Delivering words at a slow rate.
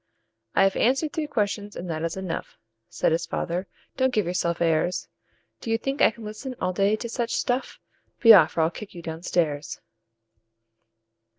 No: average, 185 wpm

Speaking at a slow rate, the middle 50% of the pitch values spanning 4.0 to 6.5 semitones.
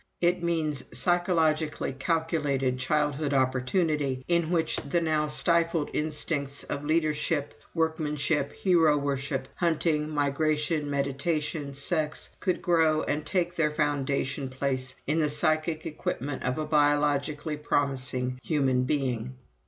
No: slow, 115 wpm; narrow, 2.4 semitones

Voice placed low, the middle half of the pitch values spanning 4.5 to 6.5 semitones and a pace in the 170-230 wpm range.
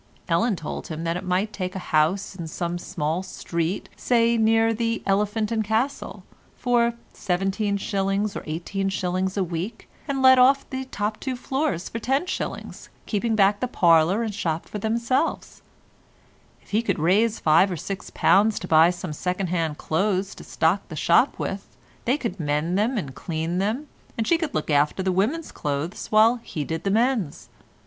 No: high, 195 Hz; average, 4.9 semitones; average, 175 wpm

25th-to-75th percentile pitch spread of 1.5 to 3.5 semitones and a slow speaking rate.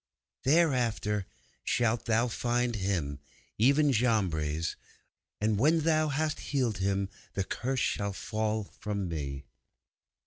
No: average, 4.8 semitones; slow, 110 wpm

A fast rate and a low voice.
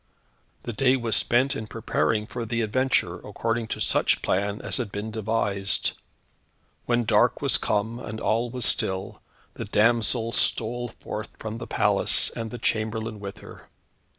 No: average, 155 wpm; low, 110 Hz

